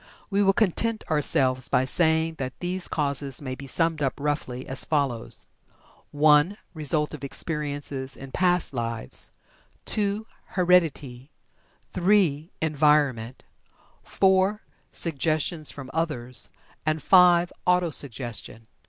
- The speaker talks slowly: Yes, slow, 110 wpm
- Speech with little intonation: No, average, 4.7 semitones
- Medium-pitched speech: Yes, medium, 150 Hz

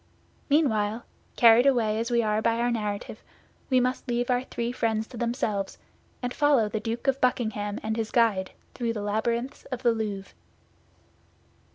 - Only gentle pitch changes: Yes, narrow, 2.3 semitones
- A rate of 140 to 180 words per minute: Yes, average, 165 wpm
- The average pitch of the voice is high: Yes, high, 230 Hz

